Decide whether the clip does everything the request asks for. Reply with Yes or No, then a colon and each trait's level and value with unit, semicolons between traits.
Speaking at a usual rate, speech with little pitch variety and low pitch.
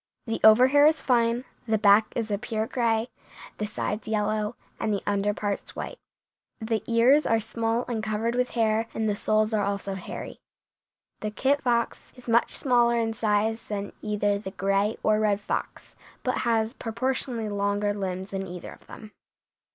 No: average, 170 wpm; narrow, 2.1 semitones; high, 220 Hz